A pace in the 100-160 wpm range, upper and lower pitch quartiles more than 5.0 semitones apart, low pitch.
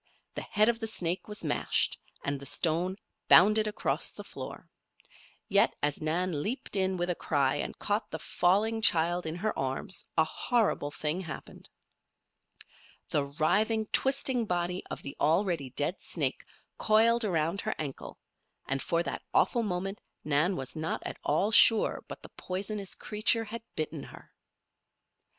No: average, 155 wpm; wide, 5.4 semitones; medium, 180 Hz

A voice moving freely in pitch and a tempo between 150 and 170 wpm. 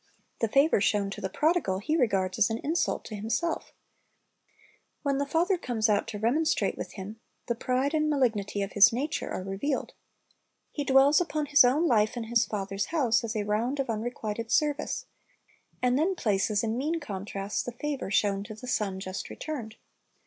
No: wide, 5.7 semitones; average, 180 wpm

